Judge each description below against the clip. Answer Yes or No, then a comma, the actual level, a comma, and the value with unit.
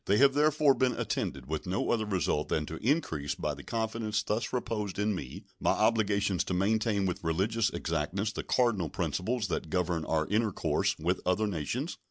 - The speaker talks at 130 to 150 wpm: No, average, 180 wpm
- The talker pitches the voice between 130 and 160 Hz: No, low, 100 Hz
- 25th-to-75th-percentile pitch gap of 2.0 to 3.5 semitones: No, average, 4.7 semitones